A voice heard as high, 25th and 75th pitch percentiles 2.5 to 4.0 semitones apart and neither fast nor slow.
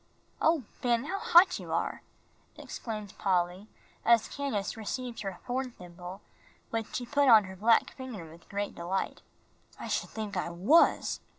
No: high, 220 Hz; average, 5.3 semitones; average, 155 wpm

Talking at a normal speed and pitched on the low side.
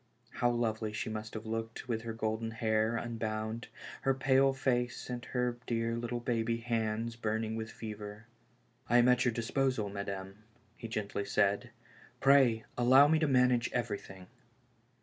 Yes: average, 155 wpm; low, 115 Hz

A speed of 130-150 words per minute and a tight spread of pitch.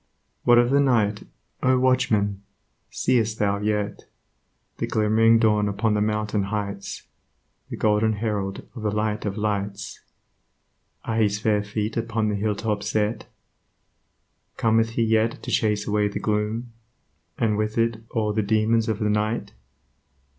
Yes: average, 145 wpm; narrow, 1.4 semitones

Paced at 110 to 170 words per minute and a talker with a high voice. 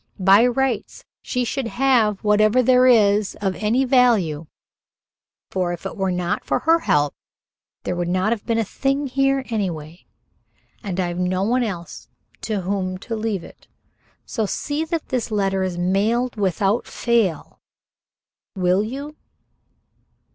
Yes: average, 145 wpm; high, 210 Hz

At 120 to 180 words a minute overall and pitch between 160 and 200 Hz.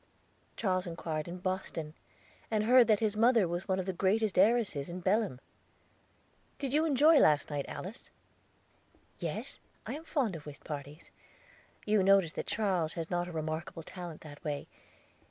Yes: average, 160 wpm; medium, 185 Hz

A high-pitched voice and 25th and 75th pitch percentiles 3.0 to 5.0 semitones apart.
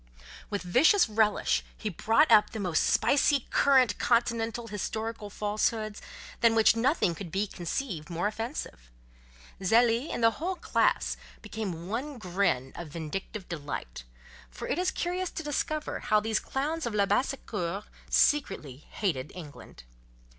No: high, 215 Hz; wide, 5.6 semitones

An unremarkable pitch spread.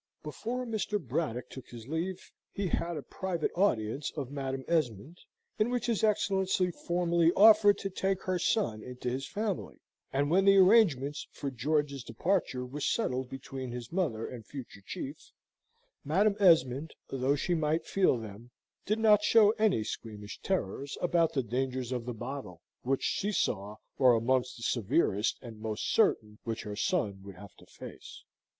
No: wide, 7.6 semitones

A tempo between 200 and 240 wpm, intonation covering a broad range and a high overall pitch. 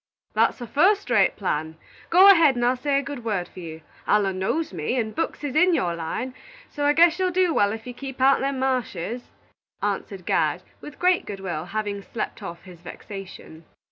Yes: fast, 205 wpm; wide, 7.1 semitones; high, 240 Hz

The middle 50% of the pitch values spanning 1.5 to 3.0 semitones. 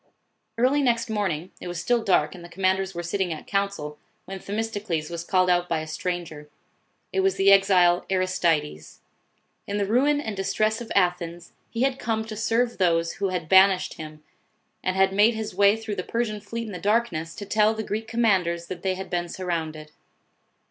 No: average, 4.0 semitones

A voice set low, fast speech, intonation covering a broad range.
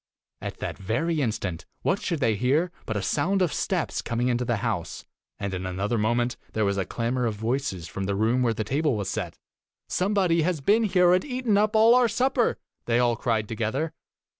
Yes: low, 120 Hz; fast, 210 wpm; wide, 8.7 semitones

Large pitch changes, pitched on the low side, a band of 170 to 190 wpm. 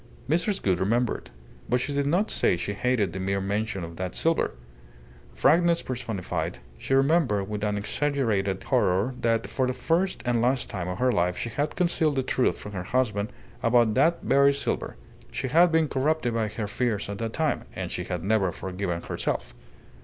Yes: wide, 6.0 semitones; low, 115 Hz; average, 185 wpm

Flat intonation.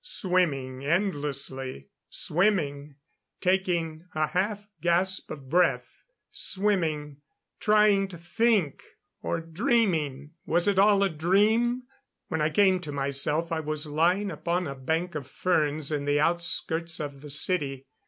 No: average, 4.4 semitones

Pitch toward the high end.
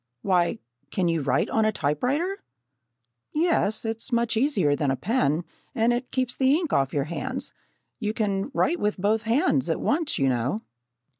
Yes: high, 220 Hz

